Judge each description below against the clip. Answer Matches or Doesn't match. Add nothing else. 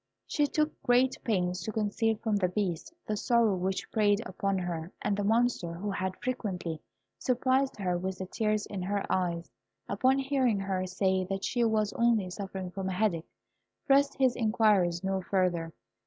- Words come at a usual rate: Matches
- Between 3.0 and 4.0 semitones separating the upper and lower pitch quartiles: Matches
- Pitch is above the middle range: Matches